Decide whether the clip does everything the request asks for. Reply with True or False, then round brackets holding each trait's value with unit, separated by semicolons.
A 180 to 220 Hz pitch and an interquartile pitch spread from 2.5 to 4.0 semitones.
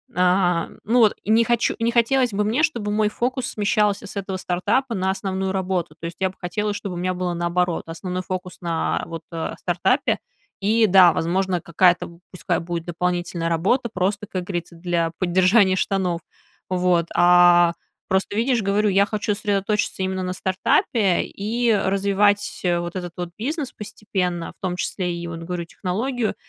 True (190 Hz; 2.9 semitones)